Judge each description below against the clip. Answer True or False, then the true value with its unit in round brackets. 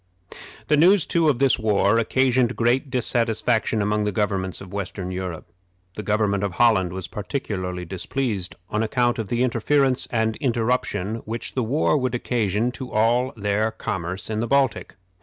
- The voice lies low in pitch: True (110 Hz)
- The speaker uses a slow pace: False (160 wpm)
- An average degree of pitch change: True (3.8 semitones)